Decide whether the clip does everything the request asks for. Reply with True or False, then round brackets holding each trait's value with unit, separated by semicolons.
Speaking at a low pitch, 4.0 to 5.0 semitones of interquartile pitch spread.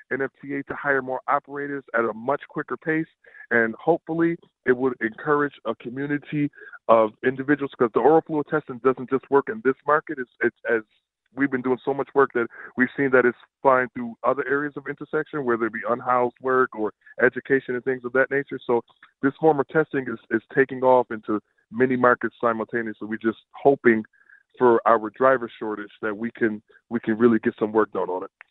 False (130 Hz; 3.2 semitones)